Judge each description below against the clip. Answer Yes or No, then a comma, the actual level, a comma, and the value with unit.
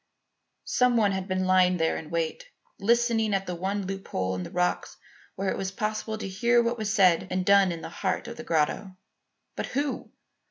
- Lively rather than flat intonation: No, average, 3.3 semitones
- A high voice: Yes, high, 195 Hz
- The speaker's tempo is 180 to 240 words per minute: Yes, average, 200 wpm